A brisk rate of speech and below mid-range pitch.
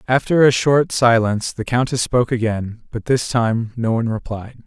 No: average, 180 wpm; low, 120 Hz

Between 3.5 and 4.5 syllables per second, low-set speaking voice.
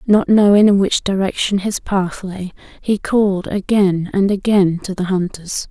No: 4.4 syllables/s; high, 195 Hz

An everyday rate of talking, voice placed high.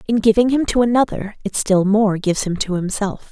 No: fast, 215 wpm; high, 210 Hz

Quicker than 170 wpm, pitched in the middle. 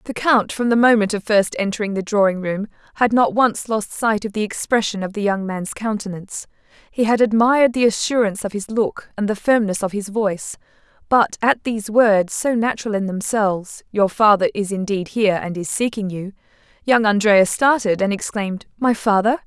No: average, 190 wpm; high, 210 Hz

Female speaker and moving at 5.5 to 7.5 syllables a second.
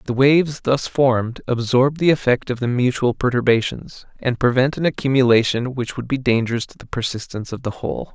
No: male; 5.7 syllables/s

